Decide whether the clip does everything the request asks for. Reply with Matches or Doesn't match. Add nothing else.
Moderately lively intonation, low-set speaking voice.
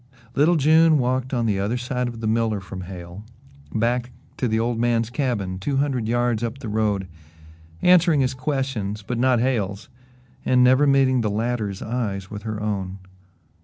Matches